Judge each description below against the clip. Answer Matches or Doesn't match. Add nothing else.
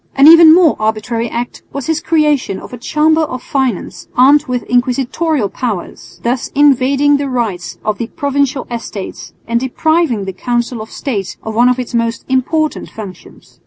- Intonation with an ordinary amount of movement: Matches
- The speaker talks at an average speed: Matches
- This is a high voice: Matches